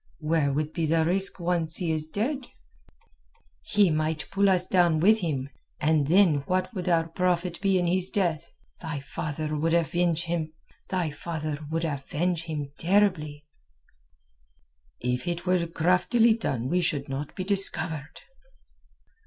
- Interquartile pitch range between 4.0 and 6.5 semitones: No, average, 2.9 semitones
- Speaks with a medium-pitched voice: Yes, medium, 165 Hz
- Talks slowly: Yes, slow, 130 wpm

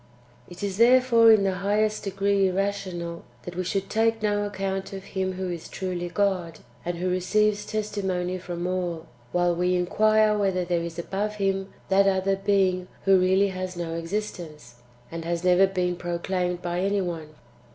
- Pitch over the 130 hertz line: Yes, medium, 185 Hz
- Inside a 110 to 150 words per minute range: No, average, 170 wpm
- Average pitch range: No, narrow, 2.2 semitones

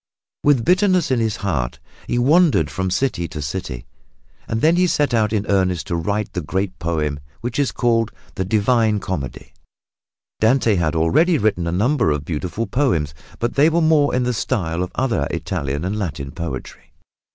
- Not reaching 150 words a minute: No, average, 175 wpm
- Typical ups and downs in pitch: No, wide, 7.1 semitones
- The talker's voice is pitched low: Yes, low, 100 Hz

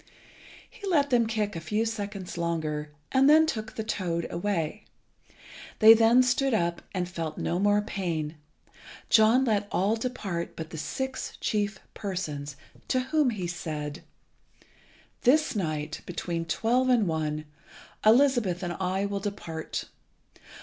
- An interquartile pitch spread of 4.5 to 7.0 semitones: Yes, average, 5.3 semitones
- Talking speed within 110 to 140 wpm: Yes, slow, 135 wpm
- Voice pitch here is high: Yes, high, 200 Hz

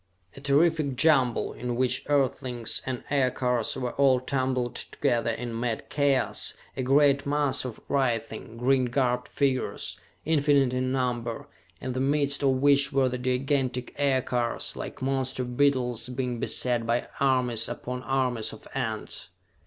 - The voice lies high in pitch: No, low, 130 Hz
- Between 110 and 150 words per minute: Yes, average, 140 wpm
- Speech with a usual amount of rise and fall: No, narrow, 2.0 semitones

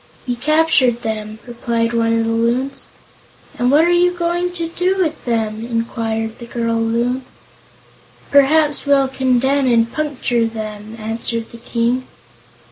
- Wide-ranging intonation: No, average, 3.8 semitones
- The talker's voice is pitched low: No, high, 240 Hz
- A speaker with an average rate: Yes, average, 145 wpm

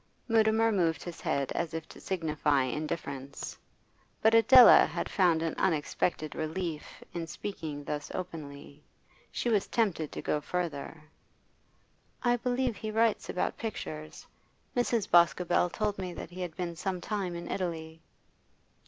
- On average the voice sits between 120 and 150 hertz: No, medium, 175 Hz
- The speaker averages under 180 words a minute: Yes, average, 140 wpm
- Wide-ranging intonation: No, average, 4.8 semitones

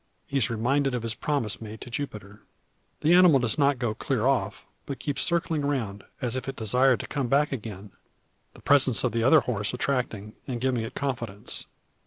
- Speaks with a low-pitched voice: Yes, low, 125 Hz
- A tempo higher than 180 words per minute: Yes, average, 195 wpm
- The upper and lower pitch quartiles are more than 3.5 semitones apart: Yes, average, 4.0 semitones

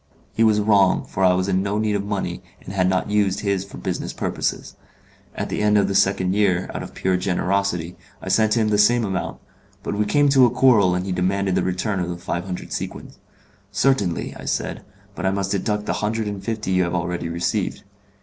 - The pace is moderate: No, fast, 220 wpm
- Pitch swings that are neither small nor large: No, narrow, 2.2 semitones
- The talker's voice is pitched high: No, low, 100 Hz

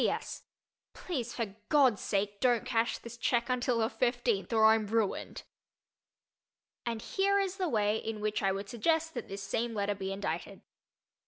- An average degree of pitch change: Yes, average, 3.3 semitones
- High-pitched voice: Yes, high, 230 Hz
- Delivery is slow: No, average, 175 wpm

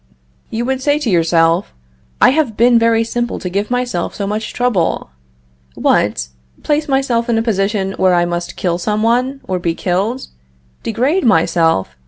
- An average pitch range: No, wide, 5.7 semitones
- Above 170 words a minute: No, average, 165 wpm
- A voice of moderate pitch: No, high, 220 Hz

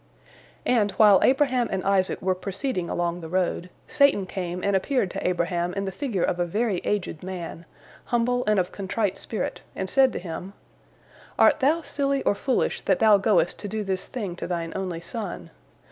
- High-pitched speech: Yes, high, 195 Hz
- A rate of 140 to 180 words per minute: No, average, 190 wpm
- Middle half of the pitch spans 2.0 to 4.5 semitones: Yes, average, 4.2 semitones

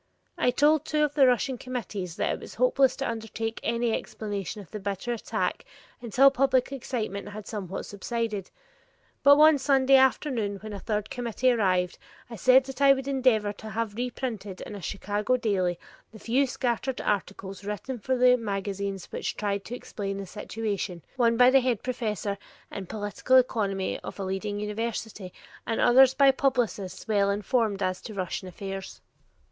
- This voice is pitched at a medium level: No, high, 220 Hz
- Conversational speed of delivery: Yes, average, 170 wpm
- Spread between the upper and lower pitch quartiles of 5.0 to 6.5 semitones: No, average, 4.2 semitones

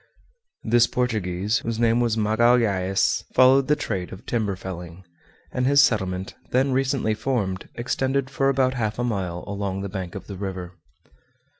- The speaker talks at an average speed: Yes, average, 155 wpm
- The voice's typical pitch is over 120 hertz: No, low, 110 Hz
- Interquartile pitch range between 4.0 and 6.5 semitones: Yes, average, 5.0 semitones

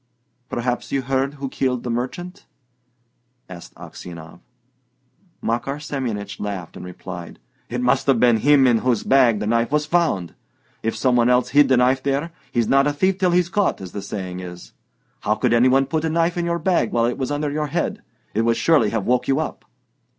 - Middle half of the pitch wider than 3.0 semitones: Yes, average, 4.5 semitones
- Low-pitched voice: Yes, low, 125 Hz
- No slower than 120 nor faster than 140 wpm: No, average, 200 wpm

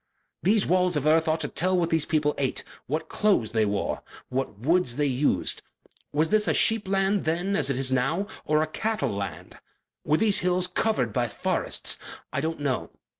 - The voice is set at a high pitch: No, medium, 155 Hz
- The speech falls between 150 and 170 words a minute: No, average, 190 wpm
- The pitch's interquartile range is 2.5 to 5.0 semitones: No, wide, 5.5 semitones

